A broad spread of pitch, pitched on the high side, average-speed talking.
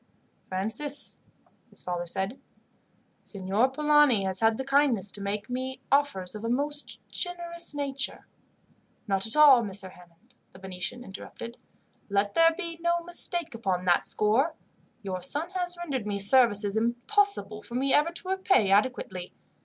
Yes: wide, 7.0 semitones; high, 240 Hz; average, 145 wpm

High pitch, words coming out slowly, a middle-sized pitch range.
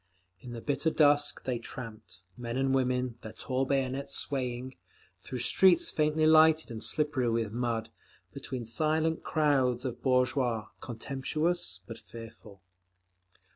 No: low, 130 Hz; slow, 130 wpm; average, 3.8 semitones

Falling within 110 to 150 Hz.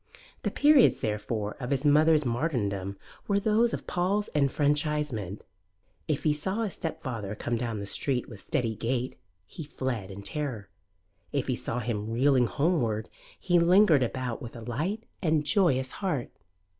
Yes: low, 135 Hz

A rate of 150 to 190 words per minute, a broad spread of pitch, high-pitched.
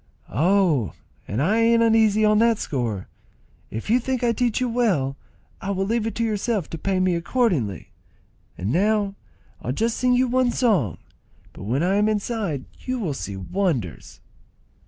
Yes: average, 165 wpm; wide, 8.3 semitones; high, 200 Hz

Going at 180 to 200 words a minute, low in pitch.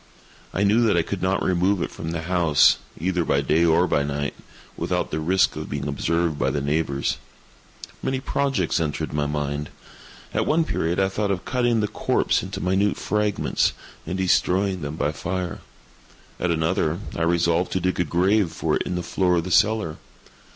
Yes: average, 185 wpm; very low, 90 Hz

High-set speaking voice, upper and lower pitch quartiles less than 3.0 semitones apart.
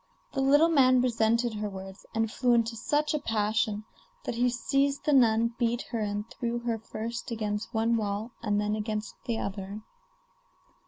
Yes: high, 230 Hz; narrow, 2.5 semitones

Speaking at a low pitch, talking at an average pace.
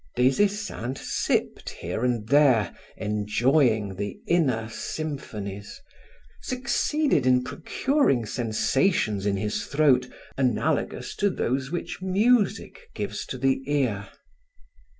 No: low, 130 Hz; slow, 105 wpm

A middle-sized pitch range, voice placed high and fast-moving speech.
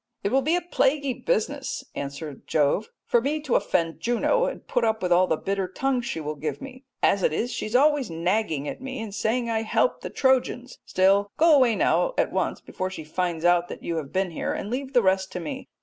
No: wide, 6.9 semitones; high, 220 Hz; fast, 230 wpm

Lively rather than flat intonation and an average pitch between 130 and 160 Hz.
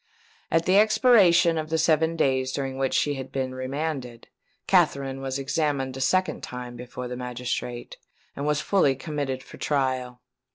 No: average, 3.5 semitones; low, 135 Hz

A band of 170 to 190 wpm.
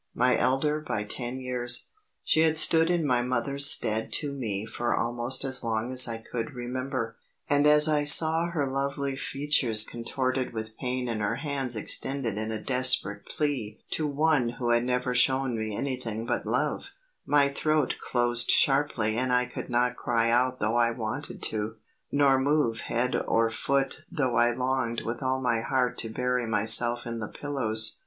Yes: average, 175 wpm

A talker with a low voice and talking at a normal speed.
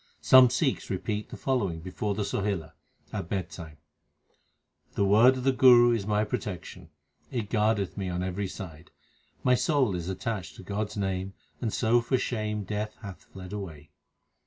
Yes: low, 105 Hz; average, 170 wpm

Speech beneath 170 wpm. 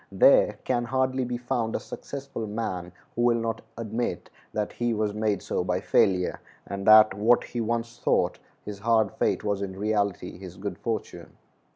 No: average, 175 wpm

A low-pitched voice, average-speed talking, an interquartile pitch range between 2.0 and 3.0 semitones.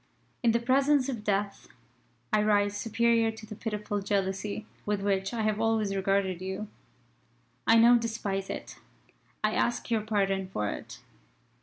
No: high, 210 Hz; average, 150 wpm; narrow, 2.4 semitones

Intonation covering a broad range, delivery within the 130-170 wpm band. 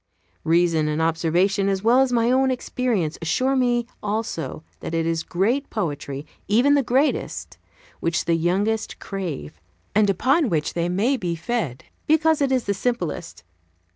Yes: wide, 6.9 semitones; average, 155 wpm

